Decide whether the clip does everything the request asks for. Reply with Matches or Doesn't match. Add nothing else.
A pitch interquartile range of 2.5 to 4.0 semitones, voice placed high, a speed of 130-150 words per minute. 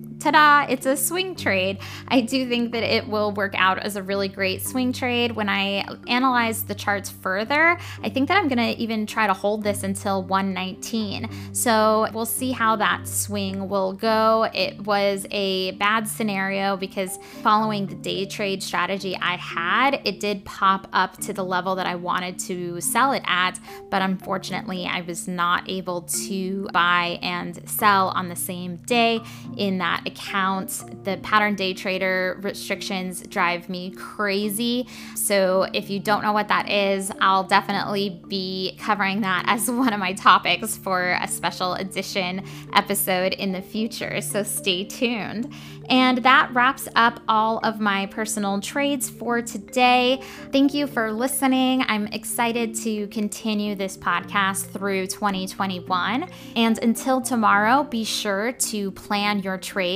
Doesn't match